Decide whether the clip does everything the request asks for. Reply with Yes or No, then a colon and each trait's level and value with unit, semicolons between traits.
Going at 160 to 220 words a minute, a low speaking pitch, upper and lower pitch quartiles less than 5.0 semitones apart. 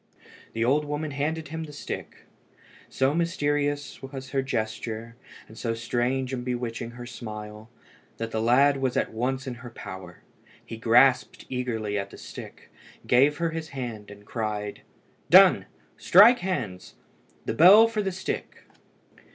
No: average, 150 wpm; low, 125 Hz; average, 4.4 semitones